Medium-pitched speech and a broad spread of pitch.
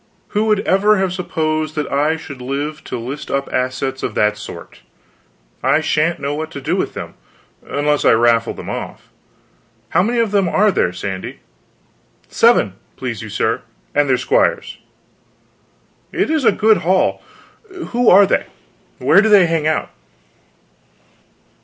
Yes: medium, 155 Hz; wide, 6.9 semitones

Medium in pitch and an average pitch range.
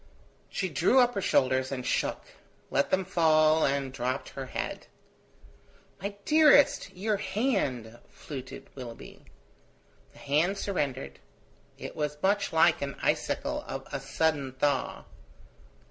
No: medium, 155 Hz; wide, 6.5 semitones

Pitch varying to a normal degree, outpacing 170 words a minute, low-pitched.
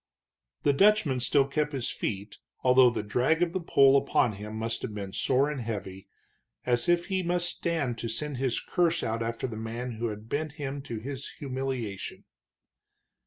Yes: average, 4.7 semitones; average, 180 wpm; low, 130 Hz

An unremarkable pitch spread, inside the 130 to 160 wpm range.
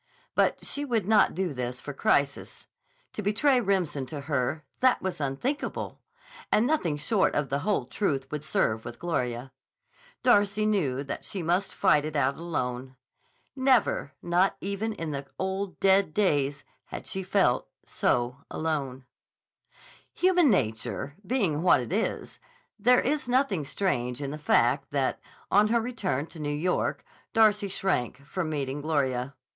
No: wide, 6.9 semitones; average, 150 wpm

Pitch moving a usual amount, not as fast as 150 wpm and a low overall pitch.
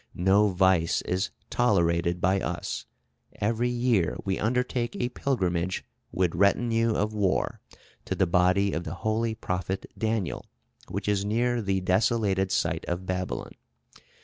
Yes: average, 3.6 semitones; slow, 135 wpm; low, 100 Hz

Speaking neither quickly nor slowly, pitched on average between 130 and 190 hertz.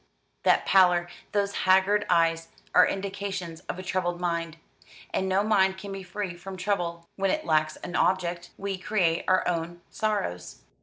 Yes: average, 160 wpm; medium, 185 Hz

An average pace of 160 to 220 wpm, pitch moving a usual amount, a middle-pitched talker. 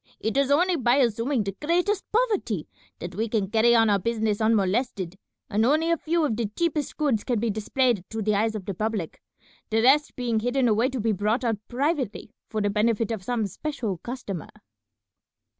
No: average, 190 wpm; average, 4.1 semitones; high, 230 Hz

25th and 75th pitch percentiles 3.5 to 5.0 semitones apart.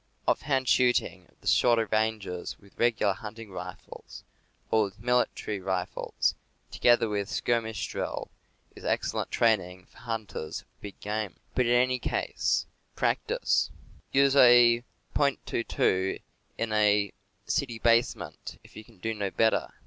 No: average, 3.1 semitones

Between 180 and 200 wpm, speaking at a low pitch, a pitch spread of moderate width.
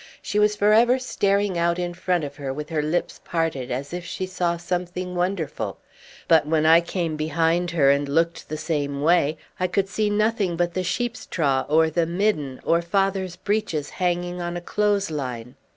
No: average, 190 wpm; medium, 175 Hz; average, 3.3 semitones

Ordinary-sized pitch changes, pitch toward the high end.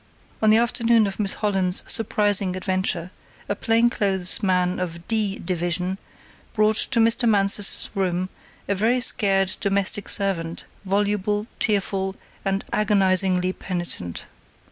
No: narrow, 2.2 semitones; high, 195 Hz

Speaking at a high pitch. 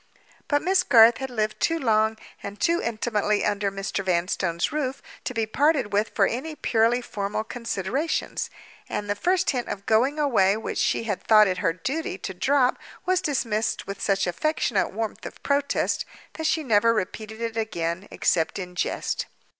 Yes: high, 220 Hz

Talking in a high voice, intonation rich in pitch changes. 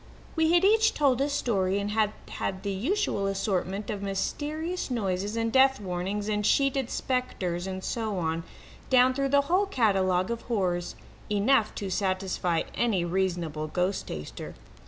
Yes: high, 205 Hz; wide, 5.8 semitones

